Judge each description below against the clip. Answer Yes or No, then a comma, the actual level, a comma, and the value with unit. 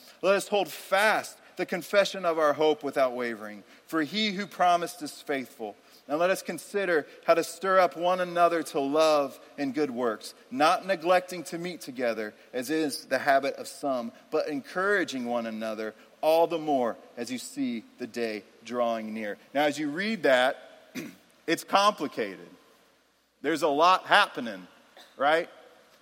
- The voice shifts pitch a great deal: Yes, wide, 5.8 semitones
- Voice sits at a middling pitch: Yes, medium, 165 Hz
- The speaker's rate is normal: Yes, average, 160 wpm